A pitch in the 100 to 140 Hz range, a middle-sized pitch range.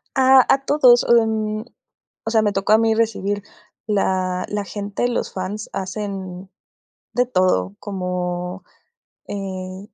No: high, 205 Hz; average, 3.1 semitones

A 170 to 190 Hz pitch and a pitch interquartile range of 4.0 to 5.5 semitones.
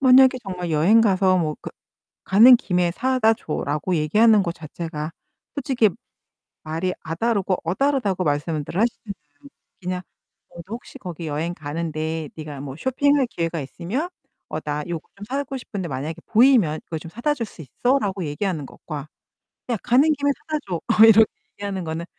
No: medium, 185 Hz; wide, 6.8 semitones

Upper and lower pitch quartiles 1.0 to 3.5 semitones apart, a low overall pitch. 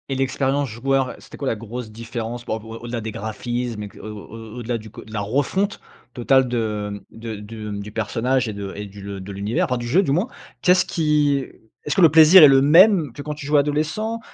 No: average, 4.8 semitones; low, 120 Hz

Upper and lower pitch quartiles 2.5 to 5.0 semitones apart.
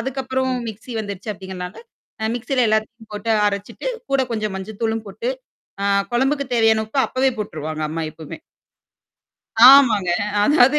Yes: average, 4.6 semitones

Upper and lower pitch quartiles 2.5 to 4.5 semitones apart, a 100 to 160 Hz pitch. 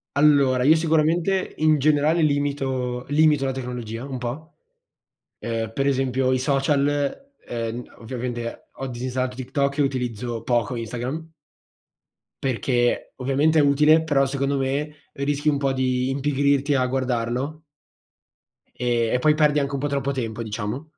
Yes: average, 2.8 semitones; low, 135 Hz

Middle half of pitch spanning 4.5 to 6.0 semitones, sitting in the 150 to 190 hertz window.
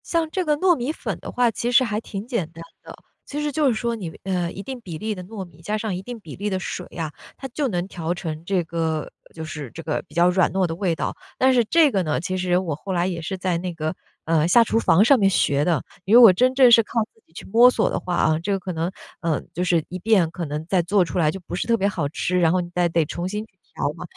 Yes: average, 5.1 semitones; medium, 185 Hz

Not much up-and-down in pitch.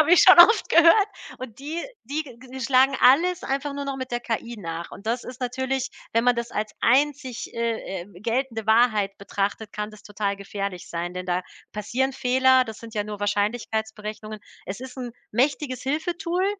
No: average, 4.1 semitones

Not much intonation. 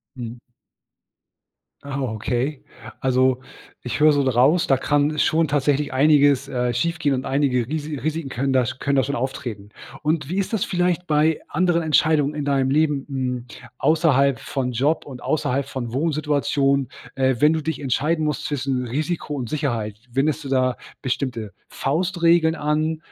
No: average, 3.0 semitones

